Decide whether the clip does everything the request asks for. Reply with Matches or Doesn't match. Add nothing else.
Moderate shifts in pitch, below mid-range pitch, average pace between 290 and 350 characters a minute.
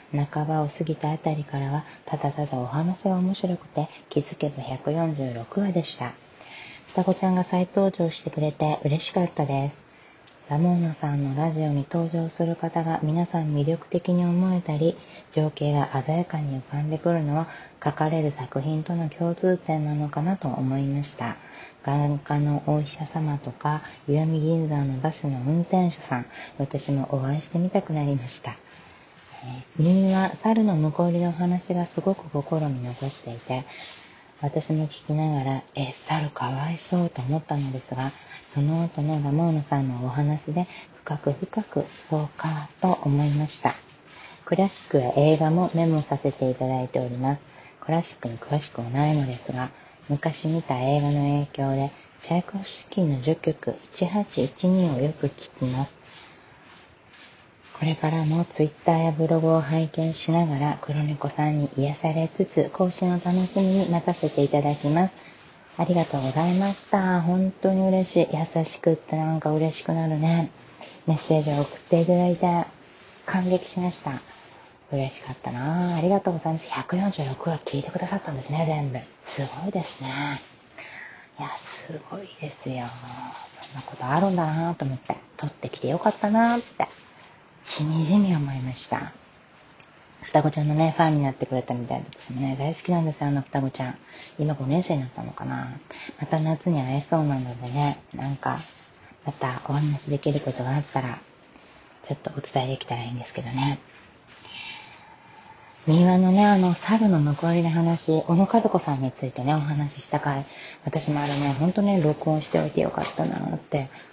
Doesn't match